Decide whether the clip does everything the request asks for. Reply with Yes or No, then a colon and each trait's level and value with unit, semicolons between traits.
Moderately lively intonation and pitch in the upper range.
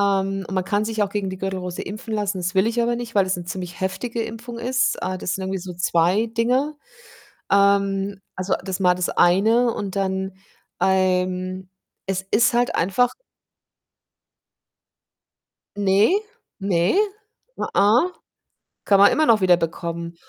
Yes: average, 3.1 semitones; high, 195 Hz